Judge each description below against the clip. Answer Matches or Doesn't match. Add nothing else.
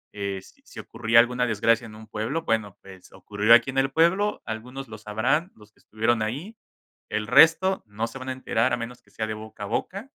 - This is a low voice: Matches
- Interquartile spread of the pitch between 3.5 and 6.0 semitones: Matches